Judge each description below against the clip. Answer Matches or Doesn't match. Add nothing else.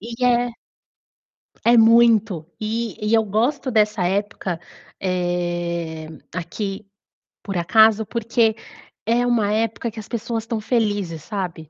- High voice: Matches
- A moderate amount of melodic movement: Matches